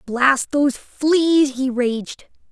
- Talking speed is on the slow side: Yes, slow, 120 wpm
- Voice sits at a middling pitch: No, very high, 270 Hz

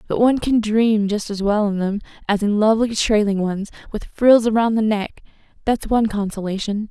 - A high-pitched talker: Yes, high, 215 Hz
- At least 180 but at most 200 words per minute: Yes, average, 190 wpm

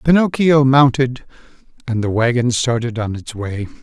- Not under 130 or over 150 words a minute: Yes, average, 140 wpm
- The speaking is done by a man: Yes, male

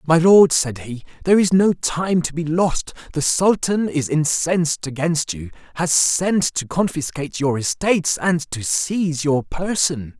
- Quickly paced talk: No, average, 165 wpm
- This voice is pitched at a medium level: Yes, medium, 160 Hz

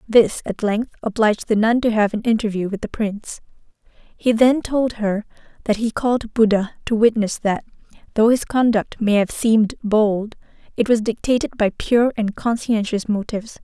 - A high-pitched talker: Yes, high, 220 Hz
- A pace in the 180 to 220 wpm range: No, average, 170 wpm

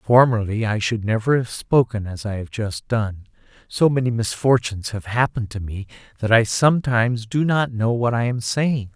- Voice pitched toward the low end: Yes, low, 115 Hz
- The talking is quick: No, average, 190 wpm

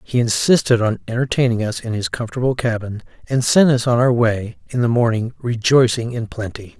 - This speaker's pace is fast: No, average, 185 wpm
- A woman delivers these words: No, male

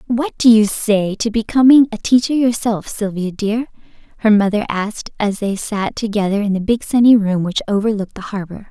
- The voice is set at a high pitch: Yes, high, 215 Hz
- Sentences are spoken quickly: No, average, 185 wpm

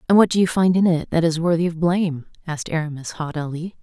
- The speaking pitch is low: No, medium, 165 Hz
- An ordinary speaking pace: No, fast, 235 wpm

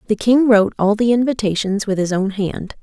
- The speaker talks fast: Yes, fast, 210 wpm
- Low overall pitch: No, high, 210 Hz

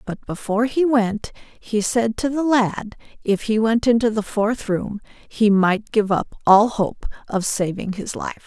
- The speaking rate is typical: Yes, average, 185 wpm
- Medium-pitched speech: No, high, 220 Hz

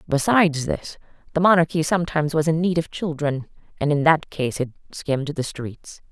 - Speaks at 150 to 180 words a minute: Yes, average, 175 wpm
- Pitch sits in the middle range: Yes, medium, 155 Hz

